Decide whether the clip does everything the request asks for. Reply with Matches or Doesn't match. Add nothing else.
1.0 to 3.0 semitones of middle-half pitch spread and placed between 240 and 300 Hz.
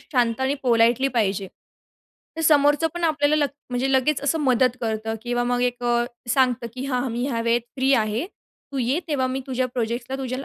Matches